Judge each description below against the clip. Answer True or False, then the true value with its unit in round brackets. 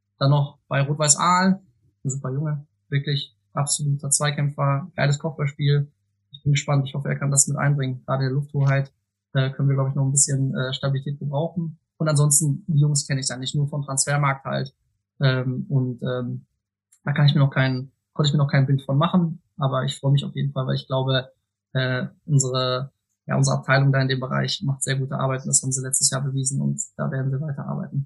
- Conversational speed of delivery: False (215 wpm)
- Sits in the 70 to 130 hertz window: False (140 Hz)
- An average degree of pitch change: False (1.8 semitones)